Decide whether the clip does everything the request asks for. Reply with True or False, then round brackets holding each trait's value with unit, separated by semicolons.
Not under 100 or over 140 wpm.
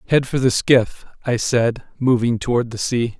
False (190 wpm)